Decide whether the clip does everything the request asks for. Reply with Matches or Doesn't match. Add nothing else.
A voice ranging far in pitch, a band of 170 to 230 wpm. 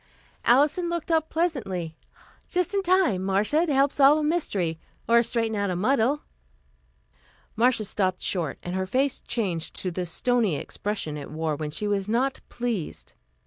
Doesn't match